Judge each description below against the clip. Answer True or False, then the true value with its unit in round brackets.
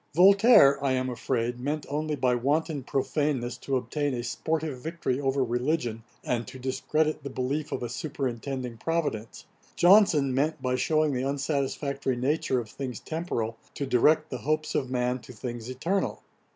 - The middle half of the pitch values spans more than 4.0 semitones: False (3.6 semitones)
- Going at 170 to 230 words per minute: False (160 wpm)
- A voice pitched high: False (135 Hz)